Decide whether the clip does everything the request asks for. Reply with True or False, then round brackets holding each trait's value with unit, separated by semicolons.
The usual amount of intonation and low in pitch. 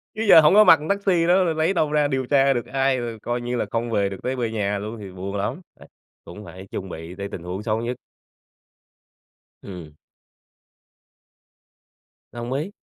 False (6.9 semitones; 120 Hz)